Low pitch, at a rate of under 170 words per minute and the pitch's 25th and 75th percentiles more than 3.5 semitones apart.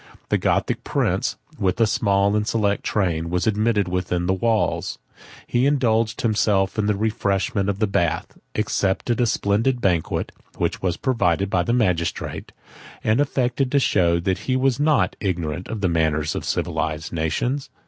Yes: low, 100 Hz; average, 160 wpm; average, 4.6 semitones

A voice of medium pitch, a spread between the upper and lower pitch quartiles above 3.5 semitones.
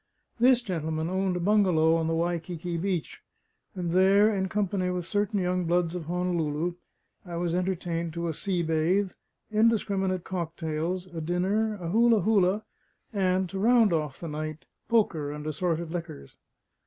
No: medium, 180 Hz; average, 2.8 semitones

